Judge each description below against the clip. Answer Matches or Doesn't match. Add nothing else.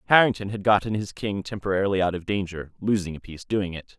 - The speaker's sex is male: Matches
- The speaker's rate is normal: Doesn't match